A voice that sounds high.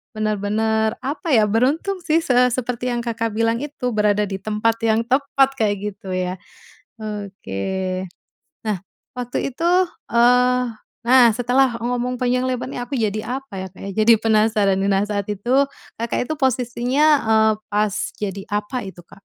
Yes: high, 230 Hz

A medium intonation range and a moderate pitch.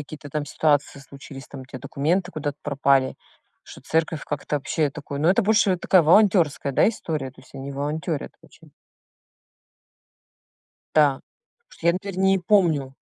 Yes: average, 4.0 semitones; medium, 150 Hz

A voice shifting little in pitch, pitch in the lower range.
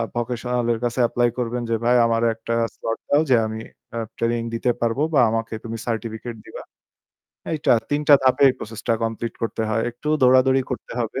Yes: narrow, 1.6 semitones; low, 115 Hz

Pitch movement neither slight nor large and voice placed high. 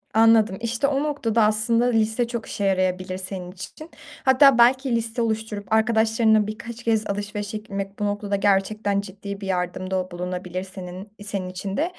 Yes: average, 3.1 semitones; high, 210 Hz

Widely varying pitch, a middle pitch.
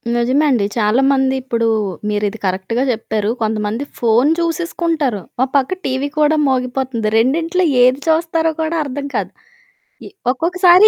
No: wide, 5.9 semitones; very high, 260 Hz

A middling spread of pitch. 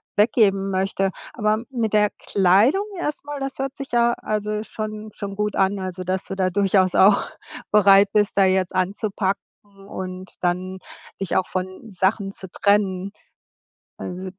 No: narrow, 2.1 semitones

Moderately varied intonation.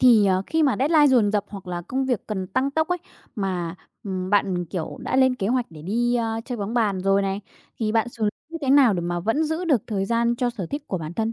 Yes: average, 5.0 semitones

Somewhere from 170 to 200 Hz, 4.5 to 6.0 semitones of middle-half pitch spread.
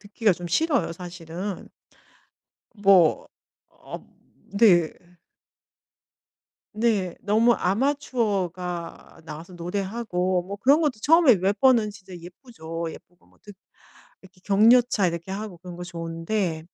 No: high, 190 Hz; average, 4.1 semitones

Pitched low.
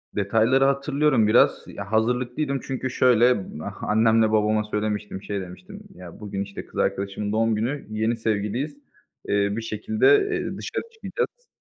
Yes: low, 110 Hz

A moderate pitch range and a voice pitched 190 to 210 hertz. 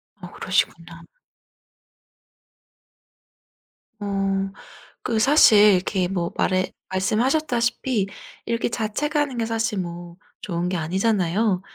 Yes: average, 4.3 semitones; high, 205 Hz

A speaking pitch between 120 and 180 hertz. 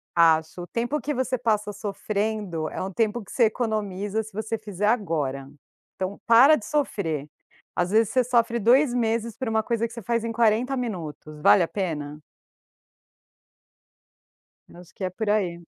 No: high, 215 Hz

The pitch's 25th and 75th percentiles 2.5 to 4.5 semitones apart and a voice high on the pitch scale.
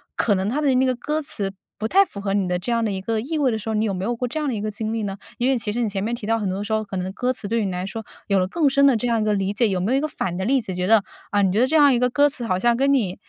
Yes: average, 4.2 semitones; high, 225 Hz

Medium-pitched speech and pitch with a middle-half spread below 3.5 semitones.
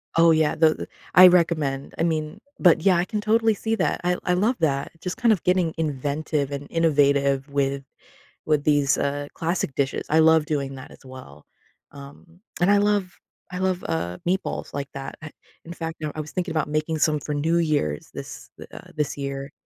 No: medium, 155 Hz; average, 3.8 semitones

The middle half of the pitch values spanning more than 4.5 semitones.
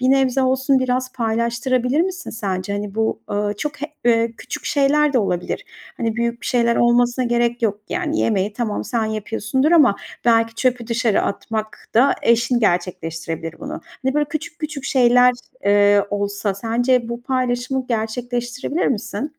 No: average, 3.1 semitones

